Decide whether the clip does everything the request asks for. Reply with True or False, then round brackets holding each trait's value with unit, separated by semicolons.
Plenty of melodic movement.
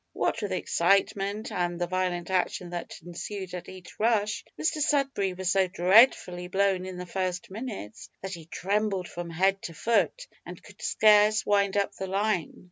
False (2.7 semitones)